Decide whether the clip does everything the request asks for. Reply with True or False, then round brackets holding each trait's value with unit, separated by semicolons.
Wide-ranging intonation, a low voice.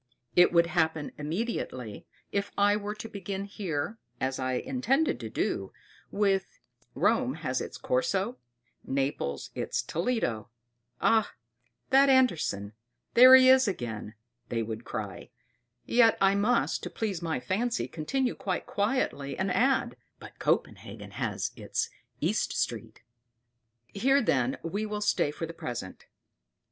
False (8.9 semitones; 195 Hz)